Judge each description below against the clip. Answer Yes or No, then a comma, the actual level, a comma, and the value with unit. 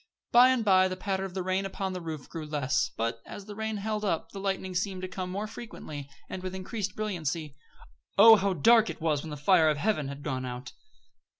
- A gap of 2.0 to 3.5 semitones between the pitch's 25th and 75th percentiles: No, average, 4.9 semitones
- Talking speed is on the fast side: Yes, fast, 225 wpm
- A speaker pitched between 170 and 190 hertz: Yes, medium, 185 Hz